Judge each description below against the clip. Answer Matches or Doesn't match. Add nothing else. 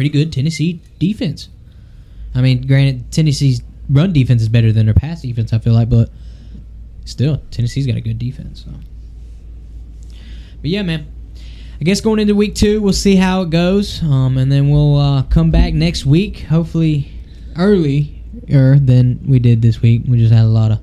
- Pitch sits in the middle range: Doesn't match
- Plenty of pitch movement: Matches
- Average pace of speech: Matches